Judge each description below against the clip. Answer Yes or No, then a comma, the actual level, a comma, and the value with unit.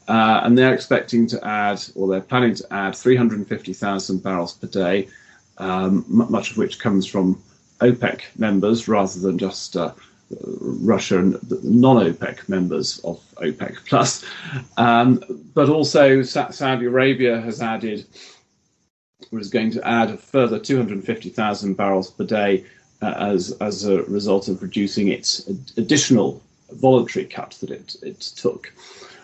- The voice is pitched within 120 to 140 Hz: No, low, 110 Hz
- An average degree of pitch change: Yes, average, 4.1 semitones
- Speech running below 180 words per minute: Yes, average, 145 wpm